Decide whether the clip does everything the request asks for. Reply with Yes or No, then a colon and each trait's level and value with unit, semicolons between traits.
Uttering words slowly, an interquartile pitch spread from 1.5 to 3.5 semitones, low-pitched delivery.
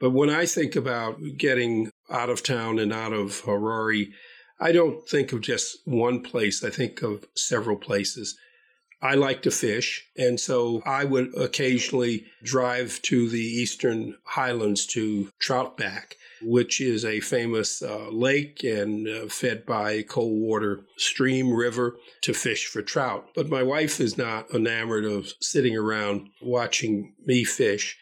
No: average, 150 wpm; average, 2.8 semitones; low, 120 Hz